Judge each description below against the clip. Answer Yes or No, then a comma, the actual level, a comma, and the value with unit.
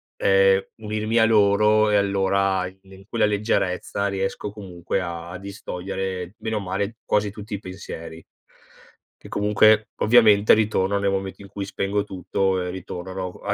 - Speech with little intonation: Yes, narrow, 1.8 semitones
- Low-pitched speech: Yes, low, 100 Hz